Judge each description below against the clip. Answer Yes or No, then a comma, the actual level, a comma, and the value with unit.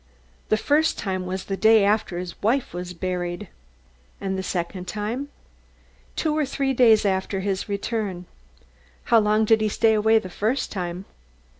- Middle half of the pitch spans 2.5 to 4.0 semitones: Yes, average, 3.2 semitones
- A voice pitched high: Yes, high, 205 Hz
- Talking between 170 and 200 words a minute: No, average, 160 wpm